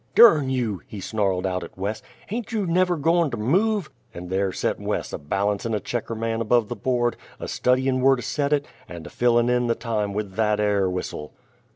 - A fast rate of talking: Yes, fast, 210 wpm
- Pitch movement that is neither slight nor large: Yes, average, 4.9 semitones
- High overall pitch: No, low, 115 Hz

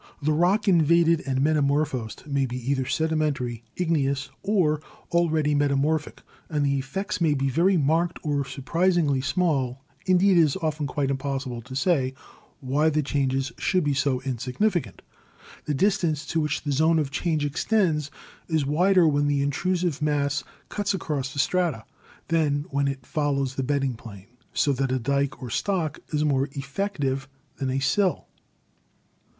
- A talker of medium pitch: Yes, medium, 145 Hz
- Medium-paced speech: Yes, average, 155 wpm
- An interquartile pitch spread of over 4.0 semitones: No, average, 3.3 semitones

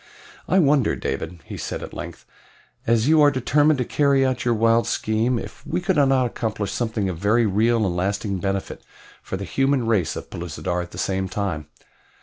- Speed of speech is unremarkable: Yes, average, 190 wpm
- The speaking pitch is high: No, low, 110 Hz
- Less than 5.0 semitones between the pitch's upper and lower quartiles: No, average, 5.3 semitones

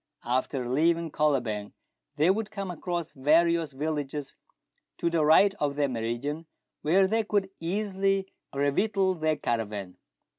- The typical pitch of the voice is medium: Yes, medium, 155 Hz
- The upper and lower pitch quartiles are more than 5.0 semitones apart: Yes, wide, 5.4 semitones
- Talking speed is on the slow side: Yes, slow, 125 wpm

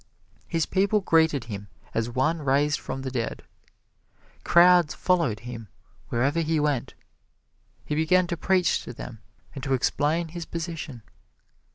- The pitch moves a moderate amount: Yes, average, 4.7 semitones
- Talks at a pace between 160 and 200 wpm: No, average, 140 wpm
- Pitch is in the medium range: Yes, medium, 150 Hz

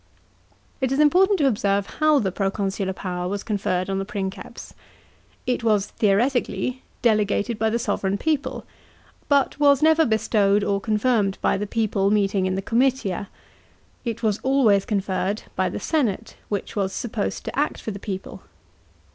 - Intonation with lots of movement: No, average, 4.3 semitones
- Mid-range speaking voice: No, high, 210 Hz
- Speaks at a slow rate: No, average, 155 wpm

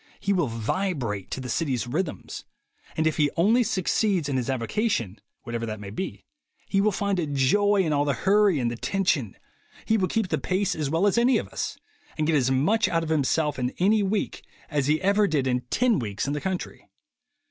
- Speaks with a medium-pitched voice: Yes, medium, 160 Hz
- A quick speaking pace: Yes, fast, 210 wpm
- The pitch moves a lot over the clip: Yes, wide, 7.1 semitones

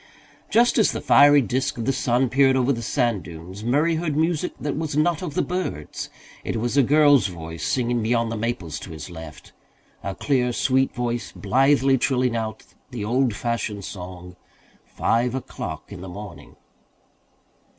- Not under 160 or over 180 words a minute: Yes, average, 170 wpm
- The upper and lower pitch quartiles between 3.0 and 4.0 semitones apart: No, average, 5.3 semitones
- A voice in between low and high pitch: No, low, 120 Hz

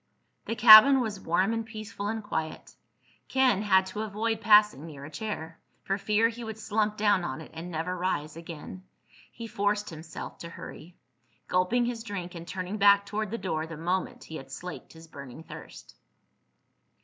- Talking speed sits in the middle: Yes, average, 175 wpm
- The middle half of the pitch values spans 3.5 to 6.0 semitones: Yes, average, 4.6 semitones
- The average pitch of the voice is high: Yes, high, 200 Hz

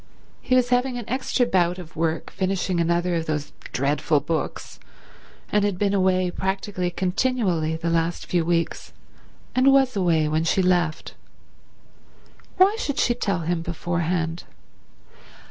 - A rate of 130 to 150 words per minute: Yes, average, 140 wpm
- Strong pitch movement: No, average, 3.7 semitones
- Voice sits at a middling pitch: Yes, medium, 180 Hz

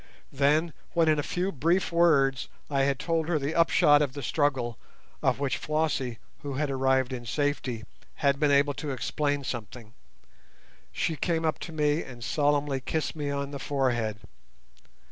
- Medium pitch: Yes, medium, 145 Hz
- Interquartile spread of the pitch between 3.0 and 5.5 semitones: No, narrow, 2.6 semitones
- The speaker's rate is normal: Yes, average, 165 wpm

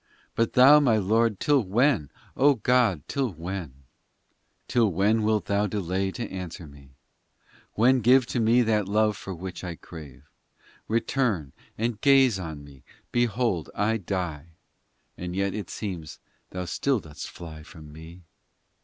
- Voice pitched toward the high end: No, low, 100 Hz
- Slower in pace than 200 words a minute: Yes, average, 150 wpm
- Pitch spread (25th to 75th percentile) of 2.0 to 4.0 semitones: No, wide, 5.4 semitones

